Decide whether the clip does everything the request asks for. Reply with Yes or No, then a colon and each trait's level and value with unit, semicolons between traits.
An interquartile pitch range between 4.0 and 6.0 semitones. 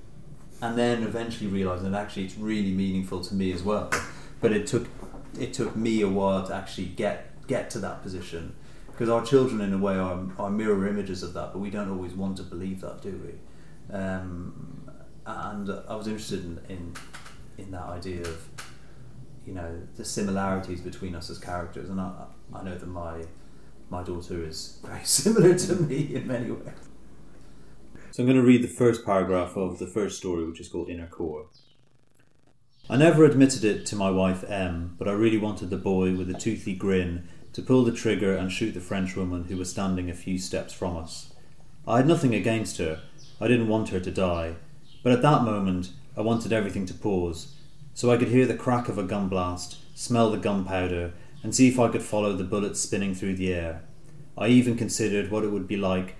Yes: average, 4.5 semitones